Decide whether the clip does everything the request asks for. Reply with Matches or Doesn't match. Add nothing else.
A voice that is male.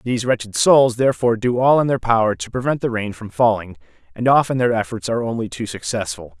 Matches